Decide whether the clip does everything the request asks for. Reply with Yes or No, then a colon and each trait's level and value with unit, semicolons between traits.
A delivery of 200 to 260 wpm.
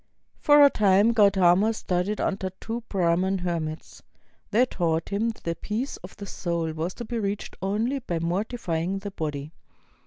No: average, 165 wpm